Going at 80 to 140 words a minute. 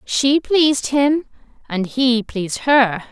Yes: slow, 135 wpm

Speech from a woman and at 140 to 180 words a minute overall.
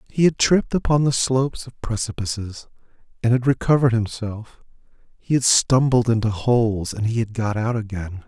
No: male; average, 160 wpm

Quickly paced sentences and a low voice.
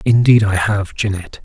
No: average, 165 wpm; low, 105 Hz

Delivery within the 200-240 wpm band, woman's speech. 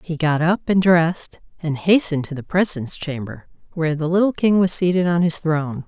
Yes: fast, 205 wpm; female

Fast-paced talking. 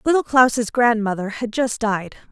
No: average, 155 wpm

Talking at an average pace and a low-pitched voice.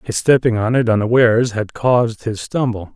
Yes: average, 180 wpm; low, 115 Hz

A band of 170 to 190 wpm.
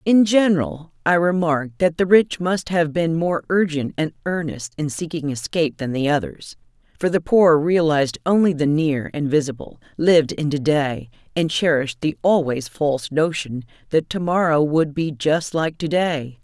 Yes: average, 175 wpm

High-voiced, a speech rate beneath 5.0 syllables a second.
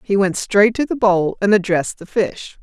Yes: high, 200 Hz; 4.8 syllables/s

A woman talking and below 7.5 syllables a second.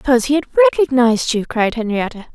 No: female; 7.9 syllables/s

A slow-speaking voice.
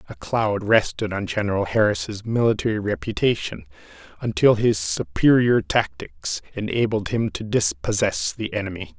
Yes: slow, 120 wpm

